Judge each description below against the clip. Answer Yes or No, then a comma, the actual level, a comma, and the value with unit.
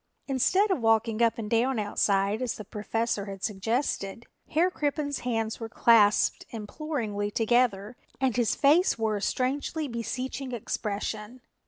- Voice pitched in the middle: No, high, 230 Hz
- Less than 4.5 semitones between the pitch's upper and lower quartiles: Yes, average, 3.7 semitones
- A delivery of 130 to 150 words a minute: Yes, average, 140 wpm